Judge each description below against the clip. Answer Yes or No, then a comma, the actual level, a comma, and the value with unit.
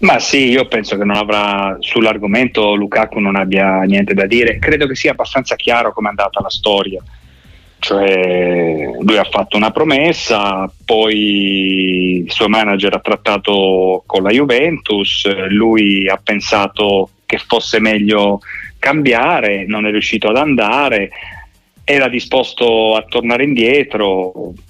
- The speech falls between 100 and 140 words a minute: Yes, average, 135 wpm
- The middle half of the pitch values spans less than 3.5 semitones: Yes, narrow, 2.4 semitones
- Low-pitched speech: Yes, low, 100 Hz